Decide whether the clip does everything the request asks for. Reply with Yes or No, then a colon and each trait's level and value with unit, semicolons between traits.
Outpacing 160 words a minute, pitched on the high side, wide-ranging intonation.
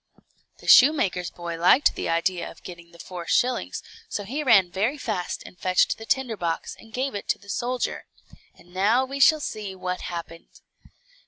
Yes: average, 180 wpm; high, 200 Hz; wide, 6.1 semitones